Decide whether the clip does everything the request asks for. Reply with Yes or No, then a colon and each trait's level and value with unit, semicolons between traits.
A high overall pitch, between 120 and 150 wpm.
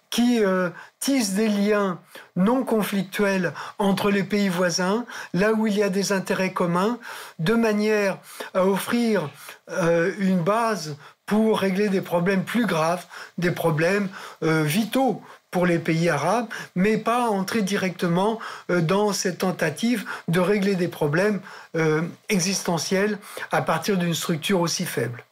Yes: high, 195 Hz; slow, 145 wpm